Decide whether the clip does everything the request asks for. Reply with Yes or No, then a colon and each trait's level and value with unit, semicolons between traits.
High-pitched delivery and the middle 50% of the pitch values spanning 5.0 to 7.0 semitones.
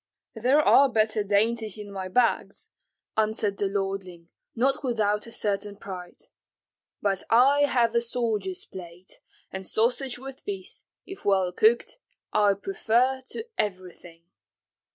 No: high, 210 Hz; average, 3.7 semitones